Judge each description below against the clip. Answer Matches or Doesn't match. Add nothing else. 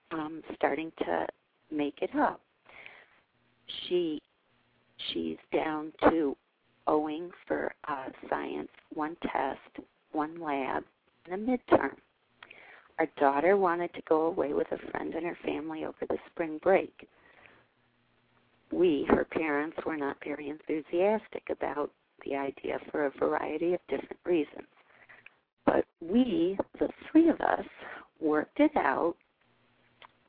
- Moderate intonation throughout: Doesn't match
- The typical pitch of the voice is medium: Matches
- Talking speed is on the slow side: Matches